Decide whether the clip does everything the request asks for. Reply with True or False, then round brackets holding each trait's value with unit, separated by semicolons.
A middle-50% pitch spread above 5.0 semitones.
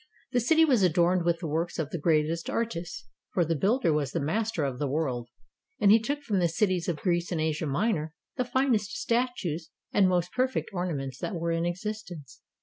True (5.4 semitones)